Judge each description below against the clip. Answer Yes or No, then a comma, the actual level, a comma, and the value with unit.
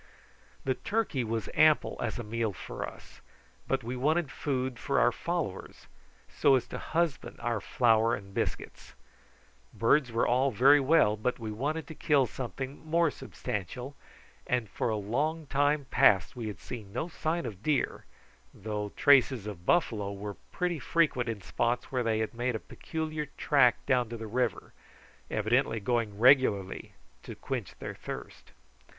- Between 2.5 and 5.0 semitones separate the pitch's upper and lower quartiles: Yes, average, 4.7 semitones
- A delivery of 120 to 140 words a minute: No, average, 160 wpm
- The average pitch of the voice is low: Yes, low, 125 Hz